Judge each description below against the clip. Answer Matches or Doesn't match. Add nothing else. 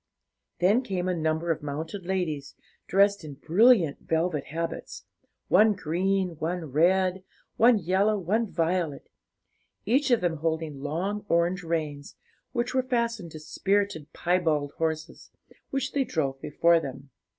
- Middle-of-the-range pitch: Matches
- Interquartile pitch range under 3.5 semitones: Doesn't match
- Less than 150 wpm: Matches